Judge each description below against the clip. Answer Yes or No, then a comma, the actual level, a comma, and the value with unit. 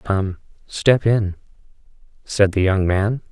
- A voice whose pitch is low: Yes, low, 100 Hz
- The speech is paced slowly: Yes, slow, 125 wpm